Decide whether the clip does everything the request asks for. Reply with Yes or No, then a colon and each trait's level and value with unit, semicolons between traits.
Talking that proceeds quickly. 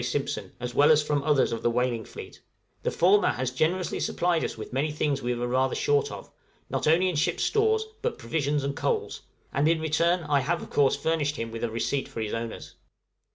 Yes: fast, 215 wpm